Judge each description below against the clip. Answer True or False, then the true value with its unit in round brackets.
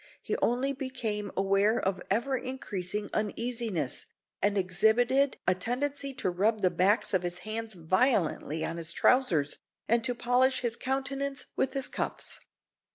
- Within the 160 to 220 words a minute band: False (145 wpm)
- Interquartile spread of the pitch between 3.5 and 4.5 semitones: False (5.5 semitones)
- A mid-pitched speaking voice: False (225 Hz)